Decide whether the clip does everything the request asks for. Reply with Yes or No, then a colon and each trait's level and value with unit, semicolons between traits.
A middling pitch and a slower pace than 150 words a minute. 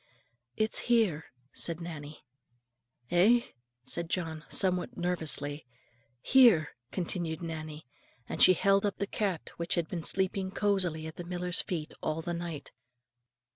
Yes: medium, 175 Hz; slow, 135 wpm